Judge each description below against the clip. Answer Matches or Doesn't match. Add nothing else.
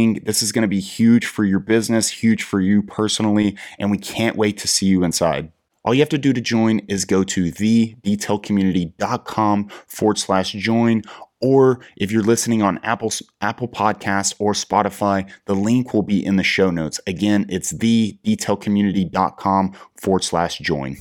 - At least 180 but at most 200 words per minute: Doesn't match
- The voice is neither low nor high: Doesn't match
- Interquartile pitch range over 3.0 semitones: Doesn't match